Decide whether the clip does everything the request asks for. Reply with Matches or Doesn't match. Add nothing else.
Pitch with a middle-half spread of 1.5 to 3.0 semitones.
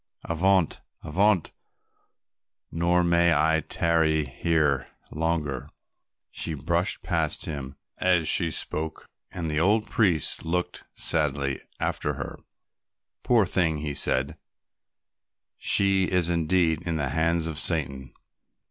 Matches